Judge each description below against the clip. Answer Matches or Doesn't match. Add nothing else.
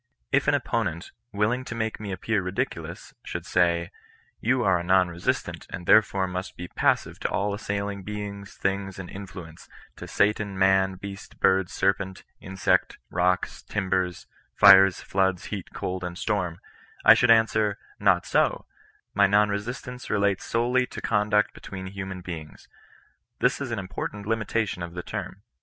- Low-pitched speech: Matches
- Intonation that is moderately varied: Doesn't match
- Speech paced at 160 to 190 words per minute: Matches